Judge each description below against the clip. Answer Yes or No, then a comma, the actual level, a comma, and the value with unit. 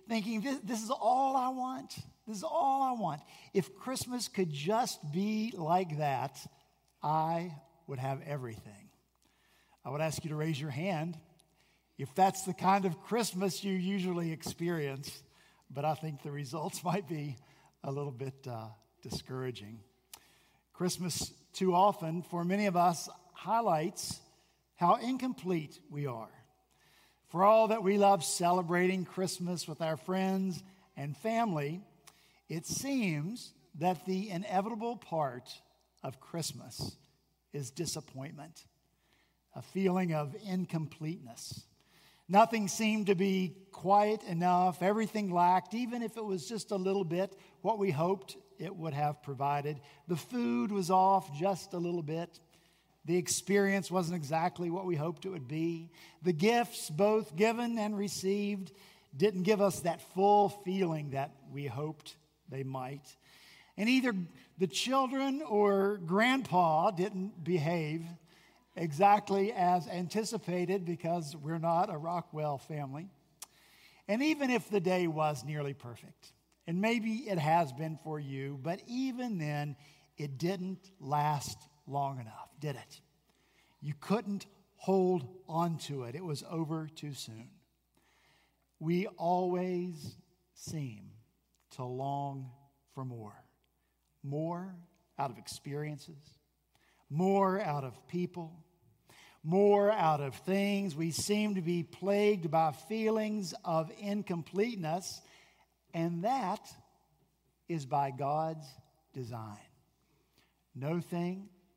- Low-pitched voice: No, medium, 175 Hz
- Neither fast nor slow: No, slow, 125 wpm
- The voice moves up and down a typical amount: Yes, average, 4.7 semitones